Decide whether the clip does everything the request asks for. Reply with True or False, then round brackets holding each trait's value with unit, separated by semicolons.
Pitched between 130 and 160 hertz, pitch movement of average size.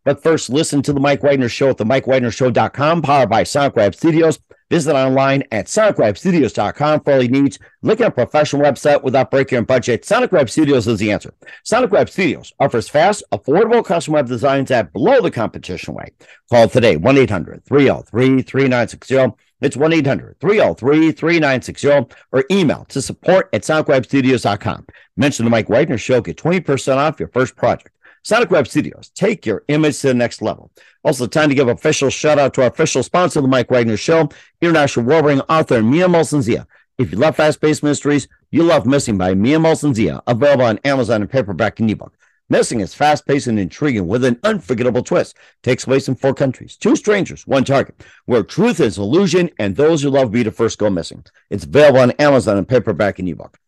True (135 Hz; 3.6 semitones)